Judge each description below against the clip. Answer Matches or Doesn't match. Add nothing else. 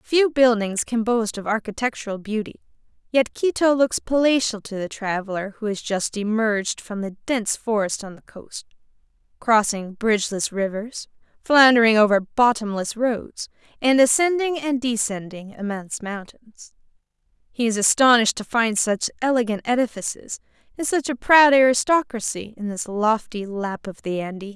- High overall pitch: Matches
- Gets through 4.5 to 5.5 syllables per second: Matches